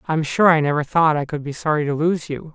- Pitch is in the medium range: Yes, medium, 155 Hz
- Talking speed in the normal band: No, fast, 305 wpm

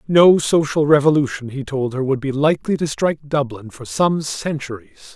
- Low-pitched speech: No, medium, 145 Hz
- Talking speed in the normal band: Yes, average, 175 wpm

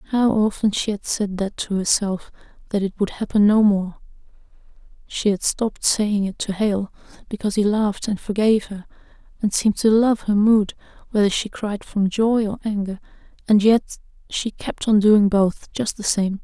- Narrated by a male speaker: No, female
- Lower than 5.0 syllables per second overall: Yes, 4.8 syllables/s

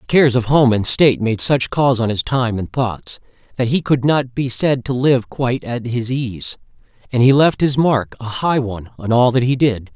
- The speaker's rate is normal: No, fast, 225 wpm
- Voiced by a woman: No, male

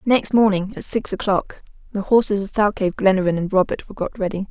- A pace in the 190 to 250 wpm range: Yes, average, 200 wpm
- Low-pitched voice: No, high, 200 Hz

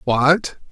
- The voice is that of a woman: No, male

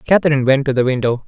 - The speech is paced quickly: Yes, fast, 235 wpm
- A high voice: No, medium, 140 Hz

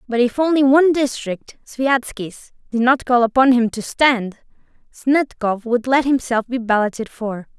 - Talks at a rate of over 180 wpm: No, average, 160 wpm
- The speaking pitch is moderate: No, high, 245 Hz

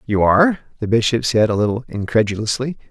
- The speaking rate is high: No, average, 165 wpm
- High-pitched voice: No, low, 115 Hz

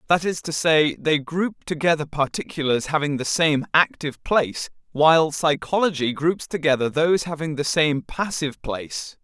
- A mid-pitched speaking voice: Yes, medium, 155 Hz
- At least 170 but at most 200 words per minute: No, average, 150 wpm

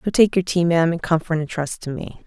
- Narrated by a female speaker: Yes, female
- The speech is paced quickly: Yes, fast, 290 wpm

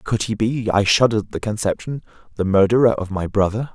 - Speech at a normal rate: No, fast, 210 wpm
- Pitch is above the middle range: No, low, 110 Hz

